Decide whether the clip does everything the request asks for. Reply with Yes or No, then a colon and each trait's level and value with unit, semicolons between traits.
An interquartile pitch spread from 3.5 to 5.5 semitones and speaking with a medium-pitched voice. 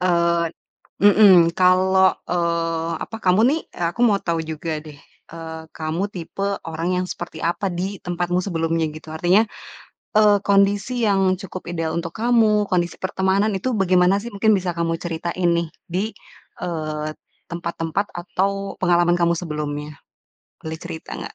No: average, 2.8 semitones; medium, 175 Hz